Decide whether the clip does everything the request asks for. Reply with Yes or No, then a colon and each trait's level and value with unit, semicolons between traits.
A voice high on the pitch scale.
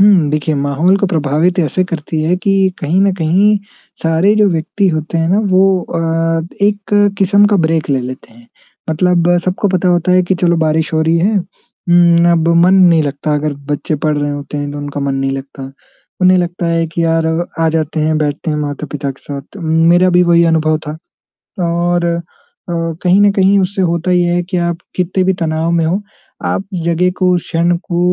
No: medium, 170 Hz